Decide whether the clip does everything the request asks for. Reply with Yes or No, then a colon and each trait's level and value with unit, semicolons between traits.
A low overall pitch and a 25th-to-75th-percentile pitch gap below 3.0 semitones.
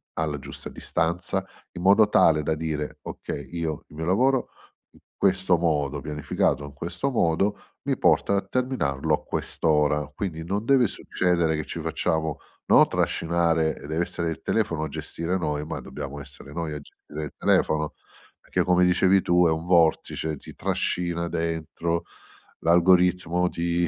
Yes: very low, 85 Hz; narrow, 2.5 semitones